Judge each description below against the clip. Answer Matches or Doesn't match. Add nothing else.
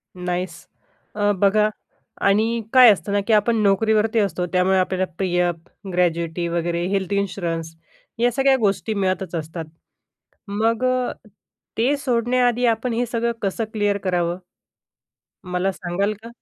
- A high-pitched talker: Matches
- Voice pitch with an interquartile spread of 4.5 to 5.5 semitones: Doesn't match